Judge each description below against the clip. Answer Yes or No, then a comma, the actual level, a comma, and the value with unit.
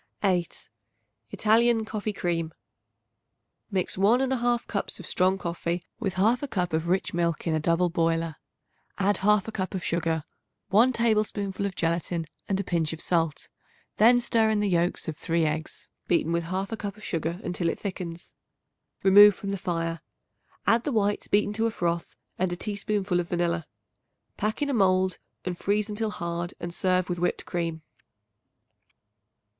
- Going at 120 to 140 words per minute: No, average, 165 wpm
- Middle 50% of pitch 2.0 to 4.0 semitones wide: Yes, average, 3.6 semitones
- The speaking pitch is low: No, medium, 185 Hz